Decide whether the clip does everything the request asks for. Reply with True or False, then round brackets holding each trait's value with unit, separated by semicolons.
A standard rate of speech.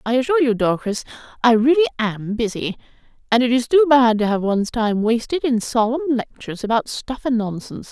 True (190 wpm)